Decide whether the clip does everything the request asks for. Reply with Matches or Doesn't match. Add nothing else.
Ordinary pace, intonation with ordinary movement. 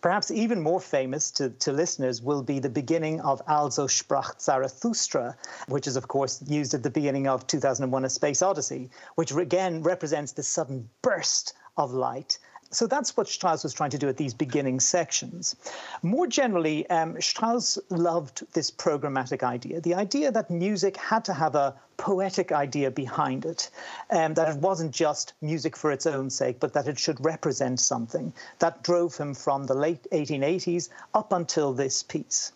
Matches